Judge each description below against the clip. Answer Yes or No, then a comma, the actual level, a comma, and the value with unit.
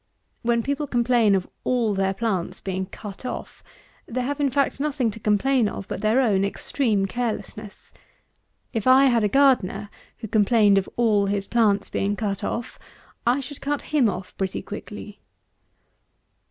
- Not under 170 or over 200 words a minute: No, average, 160 wpm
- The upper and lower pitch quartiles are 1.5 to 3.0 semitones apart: No, average, 4.1 semitones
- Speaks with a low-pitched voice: No, high, 220 Hz